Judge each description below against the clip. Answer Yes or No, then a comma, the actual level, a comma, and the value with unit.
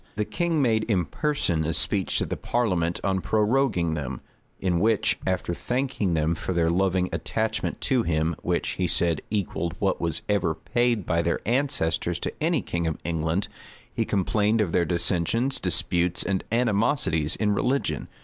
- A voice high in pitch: No, very low, 95 Hz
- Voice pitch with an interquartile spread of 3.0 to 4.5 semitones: No, average, 4.9 semitones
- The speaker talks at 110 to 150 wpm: No, average, 165 wpm